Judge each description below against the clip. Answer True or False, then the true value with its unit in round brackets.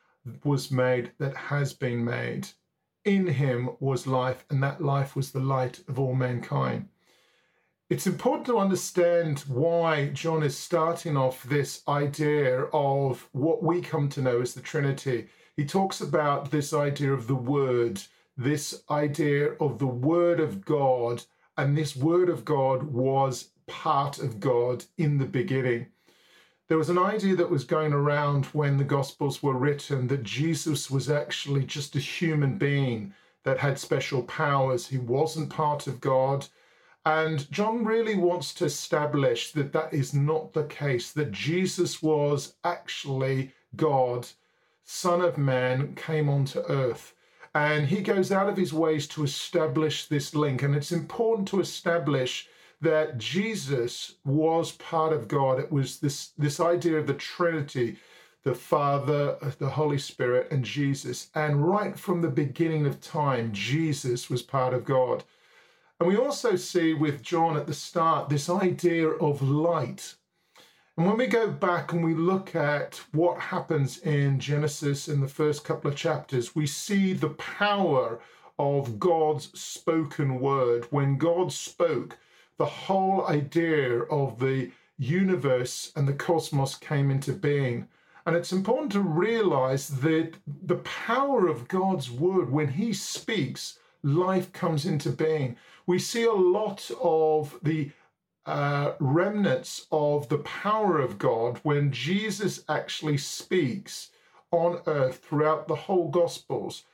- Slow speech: False (150 wpm)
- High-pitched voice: False (150 Hz)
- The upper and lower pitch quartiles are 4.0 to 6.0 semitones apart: False (3.6 semitones)